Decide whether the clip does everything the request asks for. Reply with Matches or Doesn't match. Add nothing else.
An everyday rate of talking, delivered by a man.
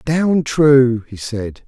Matches